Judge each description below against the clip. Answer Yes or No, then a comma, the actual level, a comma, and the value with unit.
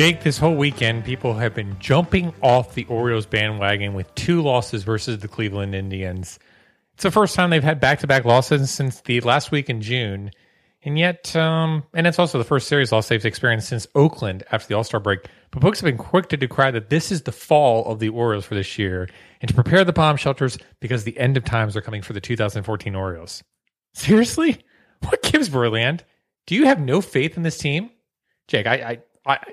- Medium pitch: No, low, 125 Hz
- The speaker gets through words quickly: Yes, fast, 215 wpm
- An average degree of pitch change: No, wide, 6.0 semitones